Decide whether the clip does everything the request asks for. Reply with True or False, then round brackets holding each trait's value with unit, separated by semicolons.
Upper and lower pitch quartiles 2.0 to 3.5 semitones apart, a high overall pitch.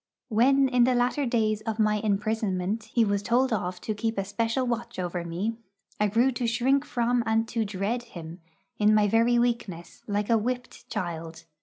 True (2.9 semitones; 220 Hz)